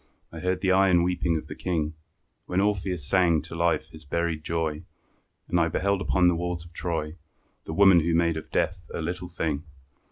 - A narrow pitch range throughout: Yes, narrow, 2.1 semitones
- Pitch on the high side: No, very low, 85 Hz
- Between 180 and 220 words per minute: Yes, average, 195 wpm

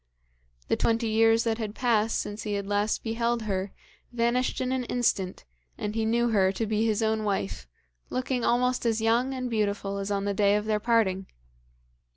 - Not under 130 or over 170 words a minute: No, average, 190 wpm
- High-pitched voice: Yes, high, 220 Hz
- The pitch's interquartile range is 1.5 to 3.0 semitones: Yes, narrow, 2.5 semitones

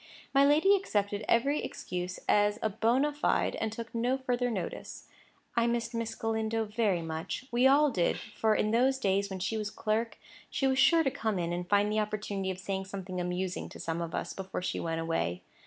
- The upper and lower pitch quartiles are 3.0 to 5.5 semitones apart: Yes, average, 4.0 semitones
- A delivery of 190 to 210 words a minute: Yes, average, 200 wpm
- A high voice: Yes, high, 215 Hz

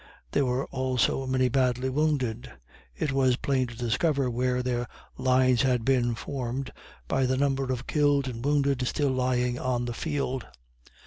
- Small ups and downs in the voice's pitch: Yes, narrow, 1.6 semitones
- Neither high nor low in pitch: No, low, 130 Hz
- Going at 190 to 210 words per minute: No, average, 155 wpm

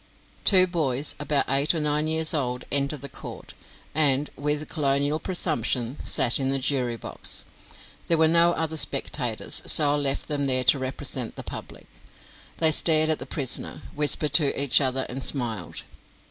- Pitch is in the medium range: Yes, medium, 145 Hz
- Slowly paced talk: No, average, 165 wpm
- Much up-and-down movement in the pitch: No, average, 2.8 semitones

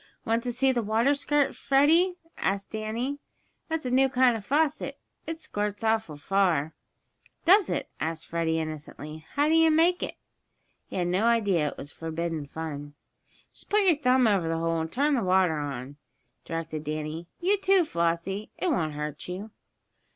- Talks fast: No, average, 175 wpm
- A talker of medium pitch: No, high, 205 Hz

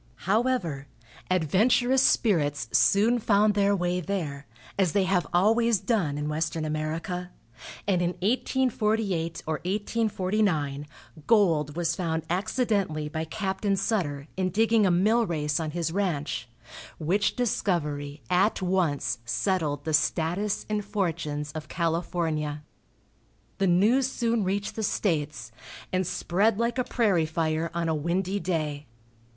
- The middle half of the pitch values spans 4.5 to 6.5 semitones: Yes, average, 4.8 semitones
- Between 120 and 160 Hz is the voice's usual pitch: No, medium, 180 Hz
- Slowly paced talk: Yes, slow, 130 wpm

